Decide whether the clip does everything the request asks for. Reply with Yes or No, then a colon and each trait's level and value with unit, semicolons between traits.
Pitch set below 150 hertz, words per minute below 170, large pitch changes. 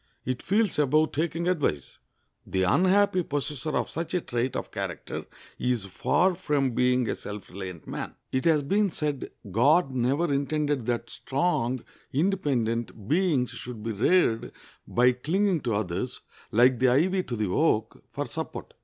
Yes: low, 135 Hz; average, 155 wpm; wide, 5.9 semitones